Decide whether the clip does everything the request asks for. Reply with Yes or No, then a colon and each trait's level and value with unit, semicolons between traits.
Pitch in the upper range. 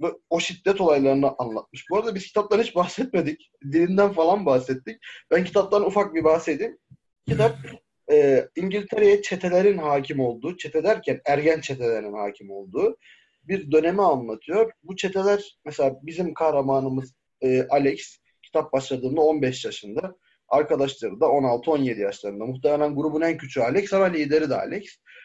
No: medium, 160 Hz